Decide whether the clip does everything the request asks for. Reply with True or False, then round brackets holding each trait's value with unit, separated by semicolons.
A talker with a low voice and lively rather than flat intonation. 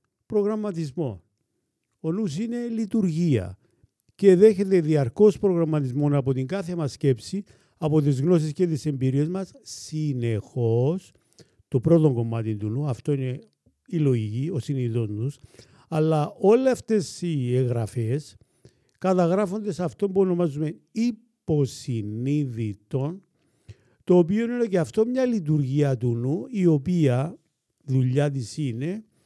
False (150 Hz; 6.3 semitones)